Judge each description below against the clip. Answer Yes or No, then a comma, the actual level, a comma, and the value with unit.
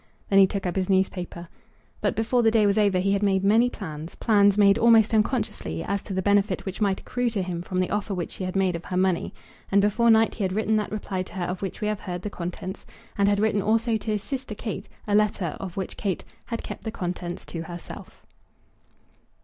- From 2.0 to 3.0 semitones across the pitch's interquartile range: Yes, narrow, 2.6 semitones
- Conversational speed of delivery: No, fast, 235 wpm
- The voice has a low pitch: No, high, 200 Hz